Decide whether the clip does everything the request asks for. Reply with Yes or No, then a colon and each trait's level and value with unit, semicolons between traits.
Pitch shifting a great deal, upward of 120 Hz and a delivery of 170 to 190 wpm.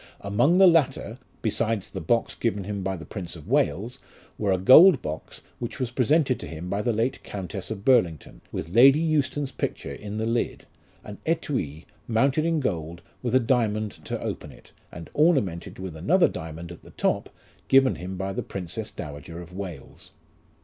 No: wide, 6.7 semitones; low, 105 Hz; average, 180 wpm